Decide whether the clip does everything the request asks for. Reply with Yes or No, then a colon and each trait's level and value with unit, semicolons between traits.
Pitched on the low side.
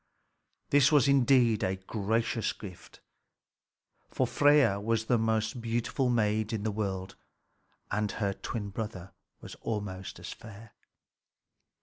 Yes: low, 110 Hz